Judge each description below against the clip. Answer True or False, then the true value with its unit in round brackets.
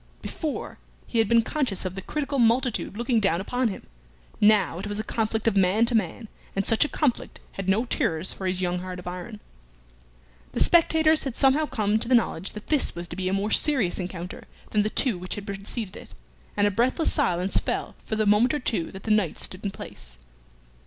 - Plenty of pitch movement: False (4.2 semitones)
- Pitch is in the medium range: False (210 Hz)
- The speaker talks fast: True (215 wpm)